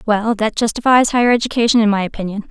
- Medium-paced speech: Yes, average, 190 wpm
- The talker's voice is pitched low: No, high, 220 Hz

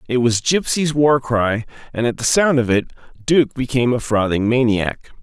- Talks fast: No, average, 185 wpm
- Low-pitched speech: Yes, low, 125 Hz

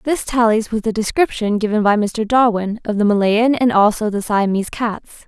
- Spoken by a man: No, female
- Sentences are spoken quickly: No, average, 195 wpm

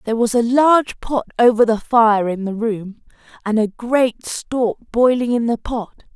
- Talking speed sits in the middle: Yes, average, 185 wpm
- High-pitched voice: Yes, high, 230 Hz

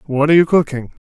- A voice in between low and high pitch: Yes, medium, 150 Hz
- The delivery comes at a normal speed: No, fast, 220 wpm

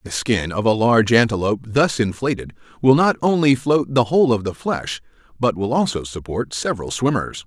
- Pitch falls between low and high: No, low, 115 Hz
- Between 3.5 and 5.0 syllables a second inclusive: No, 5.4 syllables/s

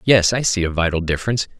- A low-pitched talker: Yes, low, 100 Hz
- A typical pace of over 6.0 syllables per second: Yes, 7.1 syllables/s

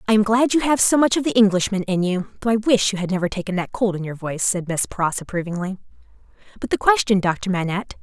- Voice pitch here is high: Yes, high, 200 Hz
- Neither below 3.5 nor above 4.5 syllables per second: No, 6.5 syllables/s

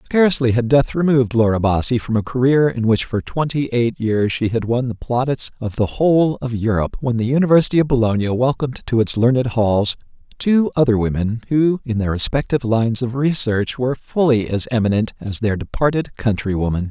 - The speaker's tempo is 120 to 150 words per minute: No, average, 190 wpm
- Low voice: Yes, low, 120 Hz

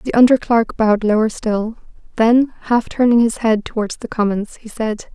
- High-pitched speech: Yes, high, 225 Hz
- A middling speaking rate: Yes, average, 185 wpm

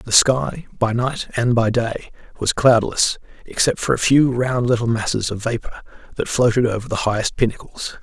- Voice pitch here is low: Yes, low, 115 Hz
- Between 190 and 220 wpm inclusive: No, average, 170 wpm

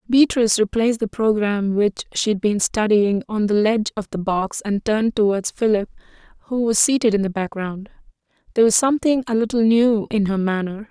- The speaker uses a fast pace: No, average, 185 wpm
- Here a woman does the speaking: Yes, female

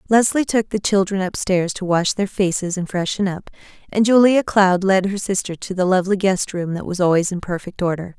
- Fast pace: Yes, fast, 220 wpm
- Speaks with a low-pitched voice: No, high, 190 Hz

